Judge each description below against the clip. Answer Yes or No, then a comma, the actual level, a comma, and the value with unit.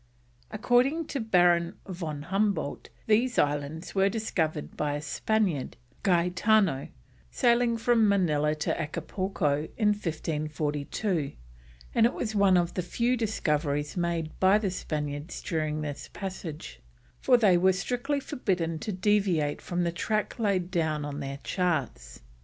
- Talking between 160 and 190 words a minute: No, slow, 135 wpm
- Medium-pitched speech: Yes, medium, 180 Hz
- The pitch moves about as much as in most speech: No, wide, 5.7 semitones